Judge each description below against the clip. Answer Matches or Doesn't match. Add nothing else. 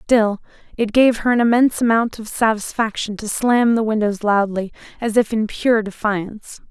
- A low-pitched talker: Doesn't match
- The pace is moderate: Matches